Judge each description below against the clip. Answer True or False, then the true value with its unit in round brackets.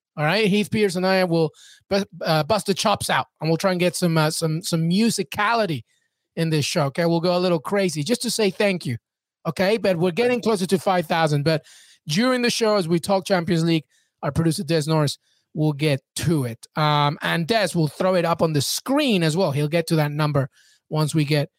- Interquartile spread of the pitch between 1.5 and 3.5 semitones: False (4.0 semitones)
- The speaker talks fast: True (220 wpm)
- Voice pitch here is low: False (170 Hz)